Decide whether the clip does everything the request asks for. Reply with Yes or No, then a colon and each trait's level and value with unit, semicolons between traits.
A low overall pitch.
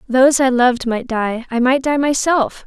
No: very high, 255 Hz